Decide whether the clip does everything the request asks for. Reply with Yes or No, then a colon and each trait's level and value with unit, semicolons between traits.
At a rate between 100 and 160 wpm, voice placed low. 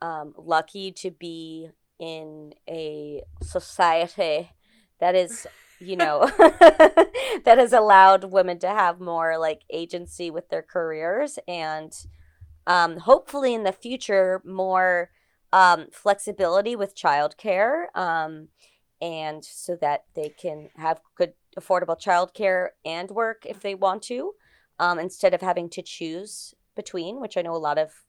No: slow, 135 wpm; medium, 180 Hz